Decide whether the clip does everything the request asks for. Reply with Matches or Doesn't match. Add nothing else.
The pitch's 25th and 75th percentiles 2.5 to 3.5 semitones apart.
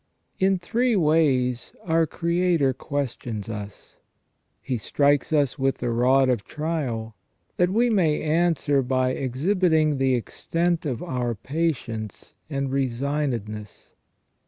Doesn't match